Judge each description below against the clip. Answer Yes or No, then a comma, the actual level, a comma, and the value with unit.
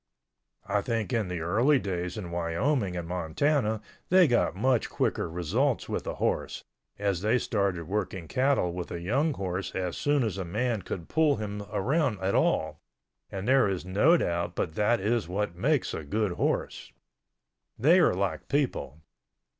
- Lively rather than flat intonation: Yes, wide, 5.9 semitones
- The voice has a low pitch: Yes, low, 100 Hz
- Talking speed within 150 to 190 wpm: Yes, average, 170 wpm